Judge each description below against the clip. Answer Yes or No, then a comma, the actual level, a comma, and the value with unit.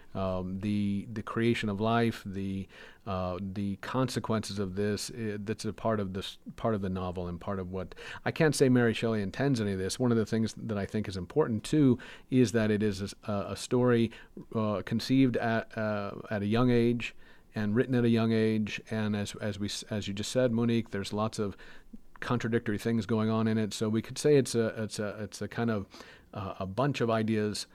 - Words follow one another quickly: Yes, fast, 220 wpm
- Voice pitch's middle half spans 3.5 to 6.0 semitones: No, narrow, 2.5 semitones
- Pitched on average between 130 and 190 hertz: No, low, 110 Hz